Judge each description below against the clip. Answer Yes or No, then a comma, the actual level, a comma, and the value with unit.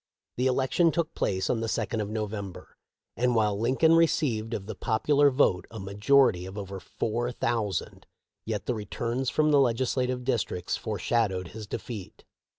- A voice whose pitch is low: Yes, low, 115 Hz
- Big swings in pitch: No, average, 4.0 semitones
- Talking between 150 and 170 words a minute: Yes, average, 160 wpm